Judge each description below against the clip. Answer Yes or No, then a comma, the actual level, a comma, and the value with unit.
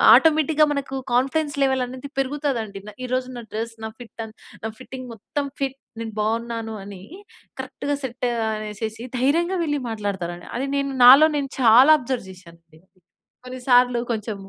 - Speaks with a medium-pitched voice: No, very high, 250 Hz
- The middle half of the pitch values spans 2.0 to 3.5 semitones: No, average, 3.9 semitones